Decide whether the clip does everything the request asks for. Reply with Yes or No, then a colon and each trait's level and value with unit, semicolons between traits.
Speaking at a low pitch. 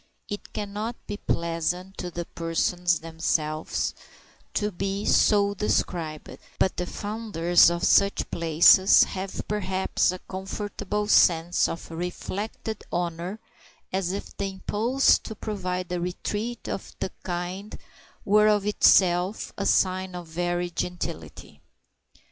No: medium, 185 Hz